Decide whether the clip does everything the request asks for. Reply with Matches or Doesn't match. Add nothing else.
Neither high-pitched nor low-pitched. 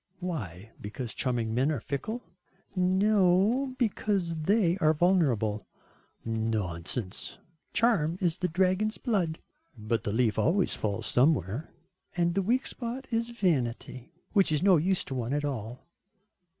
Matches